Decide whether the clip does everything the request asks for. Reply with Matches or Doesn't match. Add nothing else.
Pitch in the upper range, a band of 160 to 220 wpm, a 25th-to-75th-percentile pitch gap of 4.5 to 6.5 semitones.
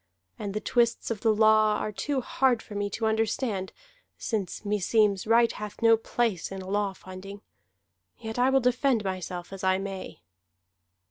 Doesn't match